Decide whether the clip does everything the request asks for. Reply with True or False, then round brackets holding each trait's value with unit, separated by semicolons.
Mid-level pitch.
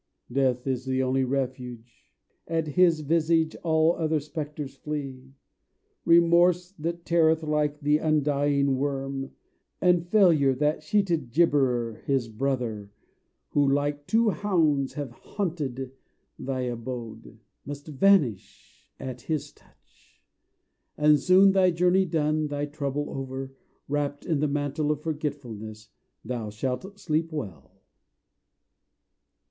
True (145 Hz)